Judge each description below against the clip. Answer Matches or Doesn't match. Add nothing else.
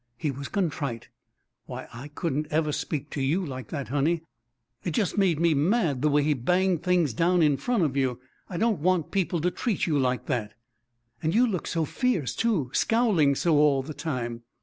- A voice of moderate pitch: Matches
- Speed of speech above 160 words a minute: Matches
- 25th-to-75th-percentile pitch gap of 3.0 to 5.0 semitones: Matches